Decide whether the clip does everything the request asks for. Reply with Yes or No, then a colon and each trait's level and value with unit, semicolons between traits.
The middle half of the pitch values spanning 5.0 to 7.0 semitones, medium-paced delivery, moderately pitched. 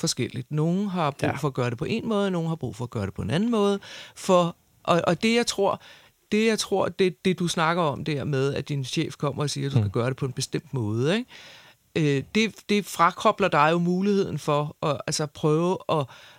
No: average, 5.3 semitones; fast, 240 wpm; medium, 160 Hz